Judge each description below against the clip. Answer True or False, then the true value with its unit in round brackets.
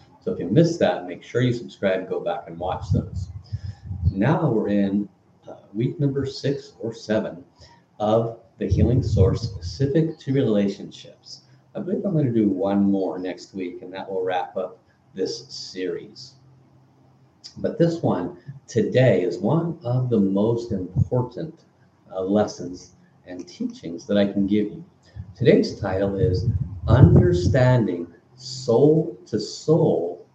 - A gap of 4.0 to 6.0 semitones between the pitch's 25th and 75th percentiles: True (5.2 semitones)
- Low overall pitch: True (110 Hz)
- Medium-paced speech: True (145 wpm)